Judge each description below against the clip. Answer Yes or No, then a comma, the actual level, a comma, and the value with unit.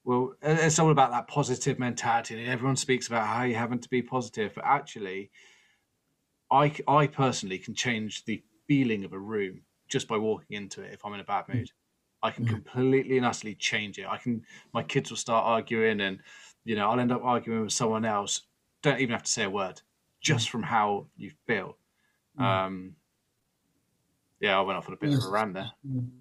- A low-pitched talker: Yes, low, 120 Hz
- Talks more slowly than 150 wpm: No, average, 200 wpm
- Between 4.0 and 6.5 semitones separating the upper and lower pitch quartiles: No, average, 3.0 semitones